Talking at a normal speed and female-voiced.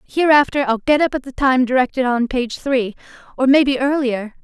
Yes: average, 190 wpm; female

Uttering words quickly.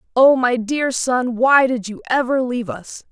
No: average, 195 wpm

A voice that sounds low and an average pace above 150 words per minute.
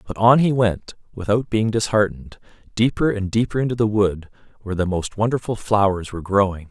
Yes: low, 105 Hz; average, 180 wpm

